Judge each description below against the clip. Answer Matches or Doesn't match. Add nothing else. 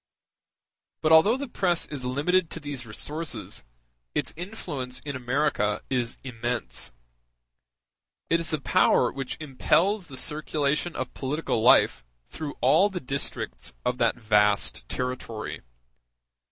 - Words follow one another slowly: Matches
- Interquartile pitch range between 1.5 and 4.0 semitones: Doesn't match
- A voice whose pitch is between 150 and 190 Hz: Doesn't match